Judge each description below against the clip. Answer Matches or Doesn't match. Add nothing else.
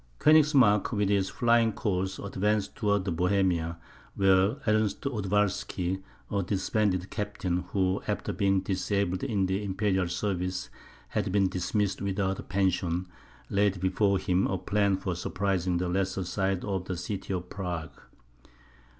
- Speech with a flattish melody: Matches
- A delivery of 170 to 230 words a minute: Doesn't match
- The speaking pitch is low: Matches